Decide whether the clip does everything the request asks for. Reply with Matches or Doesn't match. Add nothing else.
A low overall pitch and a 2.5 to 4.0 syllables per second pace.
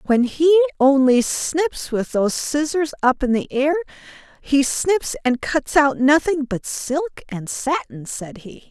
Doesn't match